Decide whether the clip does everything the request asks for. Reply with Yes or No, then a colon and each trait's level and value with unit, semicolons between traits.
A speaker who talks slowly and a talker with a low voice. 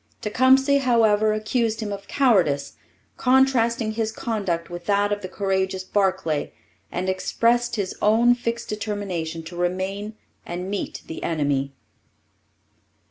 No: slow, 125 wpm; high, 205 Hz